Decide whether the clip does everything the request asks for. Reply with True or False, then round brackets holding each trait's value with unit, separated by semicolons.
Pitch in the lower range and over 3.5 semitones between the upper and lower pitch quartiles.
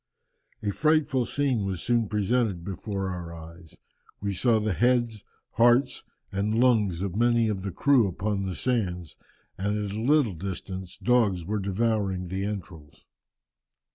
True (105 Hz; 4.0 semitones)